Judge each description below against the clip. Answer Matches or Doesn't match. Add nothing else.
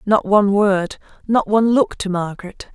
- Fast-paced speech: Doesn't match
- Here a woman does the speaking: Matches